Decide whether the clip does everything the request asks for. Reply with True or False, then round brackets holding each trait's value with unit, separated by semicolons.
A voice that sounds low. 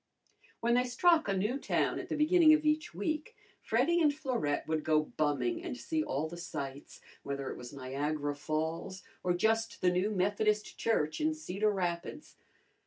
False (195 Hz)